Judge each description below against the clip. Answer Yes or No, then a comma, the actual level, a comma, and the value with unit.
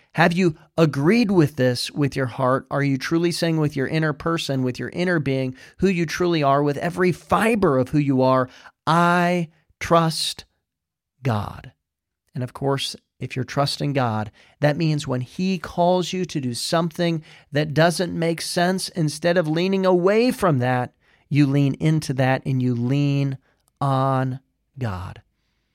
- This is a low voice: No, medium, 145 Hz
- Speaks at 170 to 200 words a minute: No, average, 160 wpm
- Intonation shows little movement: No, average, 4.6 semitones